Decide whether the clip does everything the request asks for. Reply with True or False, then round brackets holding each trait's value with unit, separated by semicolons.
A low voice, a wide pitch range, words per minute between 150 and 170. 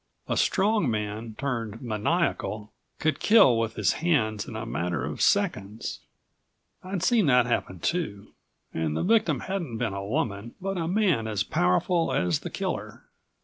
True (115 Hz; 8.6 semitones; 155 wpm)